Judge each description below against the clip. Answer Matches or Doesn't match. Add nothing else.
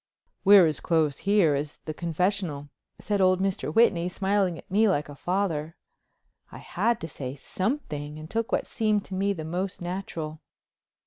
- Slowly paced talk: Doesn't match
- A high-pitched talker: Doesn't match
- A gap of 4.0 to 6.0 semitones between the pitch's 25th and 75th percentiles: Matches